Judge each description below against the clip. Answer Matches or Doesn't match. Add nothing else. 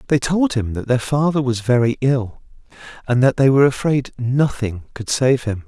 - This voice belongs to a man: Matches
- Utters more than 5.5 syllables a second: Doesn't match